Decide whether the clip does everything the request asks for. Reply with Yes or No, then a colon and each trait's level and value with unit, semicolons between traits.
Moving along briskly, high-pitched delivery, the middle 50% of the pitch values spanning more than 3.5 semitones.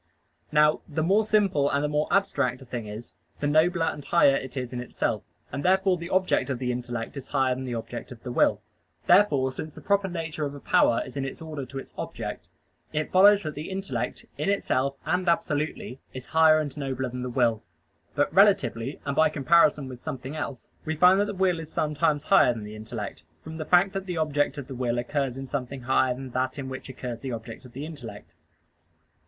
No: fast, 220 wpm; medium, 140 Hz; average, 4.3 semitones